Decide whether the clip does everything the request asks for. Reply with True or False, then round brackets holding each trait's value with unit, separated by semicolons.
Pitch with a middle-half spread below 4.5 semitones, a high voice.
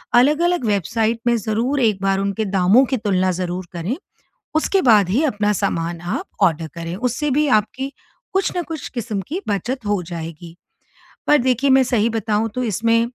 False (5.2 semitones; 220 Hz)